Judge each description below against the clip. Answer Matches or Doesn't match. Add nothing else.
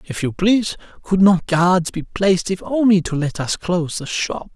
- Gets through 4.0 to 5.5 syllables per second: Matches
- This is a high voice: Doesn't match